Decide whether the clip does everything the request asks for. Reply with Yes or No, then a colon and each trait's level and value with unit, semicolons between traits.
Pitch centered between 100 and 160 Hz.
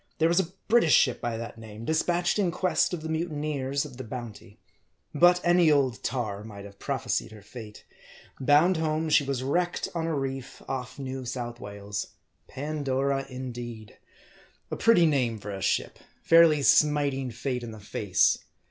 Yes: low, 135 Hz